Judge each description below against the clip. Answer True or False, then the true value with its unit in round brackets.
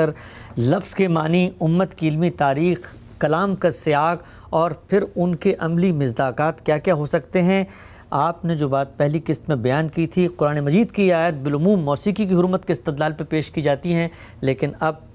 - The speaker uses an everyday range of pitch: True (3.3 semitones)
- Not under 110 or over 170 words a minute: False (190 wpm)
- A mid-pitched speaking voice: True (160 Hz)